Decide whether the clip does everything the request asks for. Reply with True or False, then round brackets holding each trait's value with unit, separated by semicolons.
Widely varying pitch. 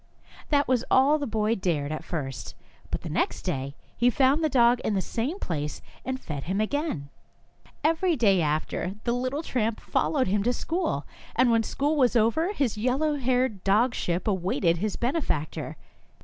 True (6.5 semitones)